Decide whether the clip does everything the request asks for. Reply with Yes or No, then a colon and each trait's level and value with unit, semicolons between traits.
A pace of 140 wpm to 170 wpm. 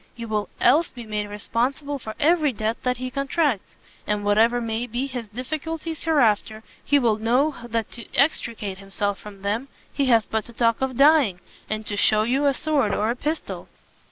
No: average, 185 wpm